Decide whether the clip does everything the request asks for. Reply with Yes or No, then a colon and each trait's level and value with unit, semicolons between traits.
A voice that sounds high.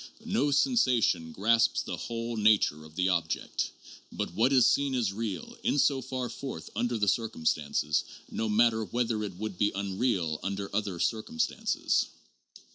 No: low, 110 Hz